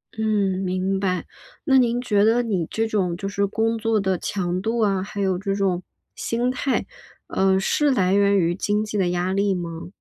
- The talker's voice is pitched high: Yes, high, 200 Hz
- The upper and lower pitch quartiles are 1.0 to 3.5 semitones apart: Yes, average, 2.9 semitones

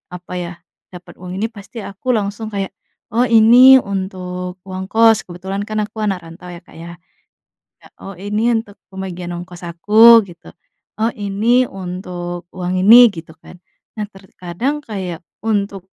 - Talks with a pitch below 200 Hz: Yes, high, 190 Hz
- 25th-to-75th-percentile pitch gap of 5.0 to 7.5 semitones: No, average, 2.7 semitones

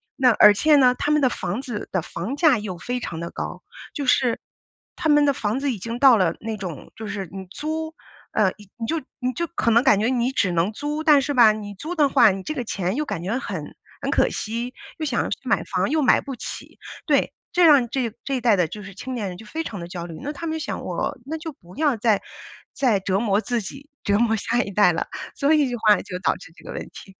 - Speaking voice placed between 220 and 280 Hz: Yes, high, 235 Hz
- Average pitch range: No, wide, 5.8 semitones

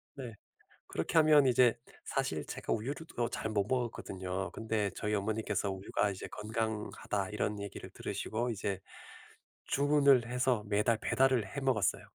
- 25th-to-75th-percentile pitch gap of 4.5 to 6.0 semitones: No, average, 3.9 semitones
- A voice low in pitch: Yes, low, 110 Hz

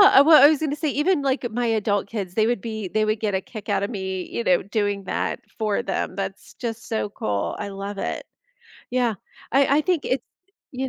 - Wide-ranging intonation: No, average, 4.7 semitones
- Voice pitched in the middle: No, high, 220 Hz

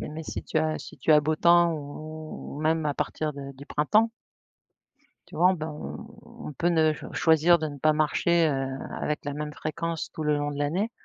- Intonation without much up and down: Yes, narrow, 2.1 semitones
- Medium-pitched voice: Yes, medium, 155 Hz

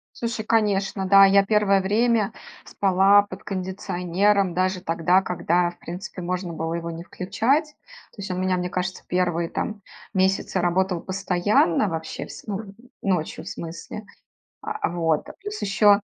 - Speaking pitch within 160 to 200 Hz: Yes, high, 190 Hz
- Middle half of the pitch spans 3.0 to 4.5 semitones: No, narrow, 2.4 semitones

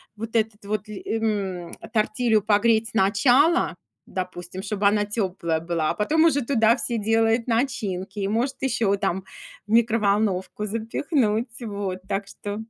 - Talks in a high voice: Yes, high, 215 Hz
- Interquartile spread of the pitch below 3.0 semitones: Yes, narrow, 2.5 semitones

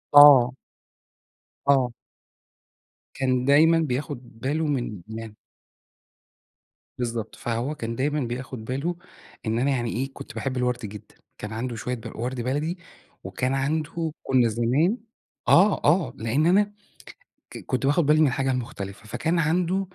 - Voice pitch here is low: Yes, low, 130 Hz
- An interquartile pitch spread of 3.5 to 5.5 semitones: Yes, average, 4.2 semitones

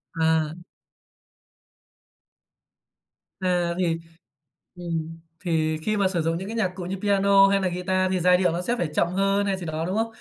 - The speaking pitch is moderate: Yes, medium, 180 Hz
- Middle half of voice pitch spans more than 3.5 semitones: No, average, 2.9 semitones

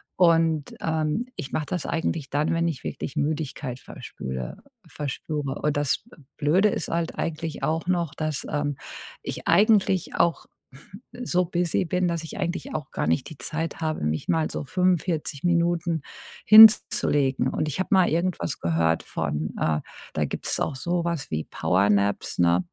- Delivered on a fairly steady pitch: No, average, 4.1 semitones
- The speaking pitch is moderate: Yes, medium, 160 Hz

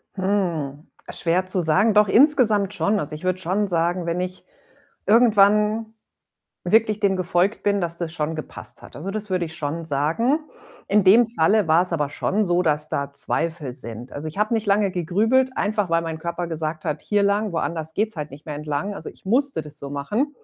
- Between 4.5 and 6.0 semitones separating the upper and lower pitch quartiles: Yes, average, 4.8 semitones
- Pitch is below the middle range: No, medium, 180 Hz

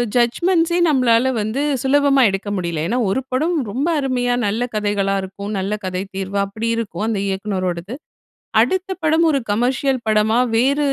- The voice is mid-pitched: No, high, 235 Hz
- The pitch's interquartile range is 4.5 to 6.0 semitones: Yes, wide, 5.4 semitones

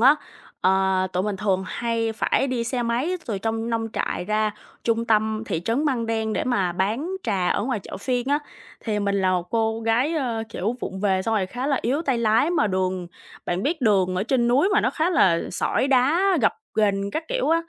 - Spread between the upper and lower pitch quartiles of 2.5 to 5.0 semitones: Yes, average, 4.5 semitones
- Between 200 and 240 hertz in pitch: Yes, high, 225 Hz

